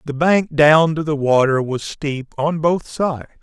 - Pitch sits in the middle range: Yes, medium, 150 Hz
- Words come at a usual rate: Yes, average, 195 wpm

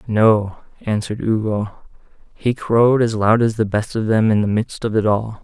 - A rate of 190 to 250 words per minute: Yes, average, 200 wpm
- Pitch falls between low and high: No, low, 110 Hz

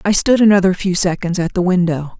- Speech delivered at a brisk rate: Yes, fast, 220 wpm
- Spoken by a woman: Yes, female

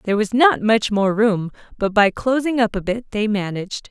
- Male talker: No, female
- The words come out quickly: Yes, fast, 215 wpm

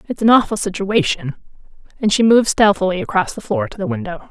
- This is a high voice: Yes, high, 200 Hz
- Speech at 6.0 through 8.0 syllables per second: Yes, 6.3 syllables/s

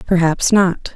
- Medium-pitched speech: Yes, medium, 180 Hz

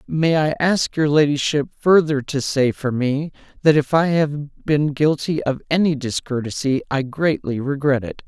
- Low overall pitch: No, medium, 145 Hz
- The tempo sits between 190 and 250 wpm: No, average, 165 wpm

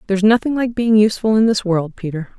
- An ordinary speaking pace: No, fast, 225 wpm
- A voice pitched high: Yes, high, 210 Hz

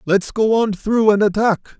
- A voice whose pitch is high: Yes, high, 210 Hz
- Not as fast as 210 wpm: Yes, average, 200 wpm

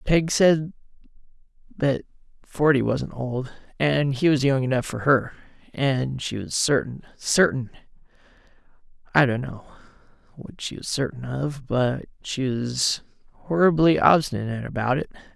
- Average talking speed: No, slow, 125 wpm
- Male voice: Yes, male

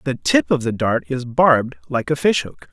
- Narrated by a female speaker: No, male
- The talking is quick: Yes, fast, 220 wpm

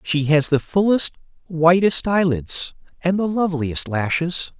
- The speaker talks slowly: Yes, slow, 130 wpm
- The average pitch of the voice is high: No, medium, 170 Hz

